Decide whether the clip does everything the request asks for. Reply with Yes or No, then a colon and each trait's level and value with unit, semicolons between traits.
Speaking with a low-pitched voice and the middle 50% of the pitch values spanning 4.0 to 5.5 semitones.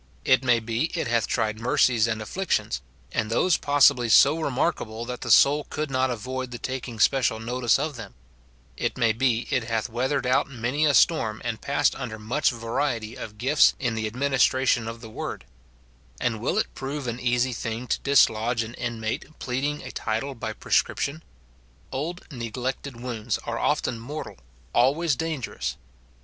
No: low, 125 Hz; average, 3.3 semitones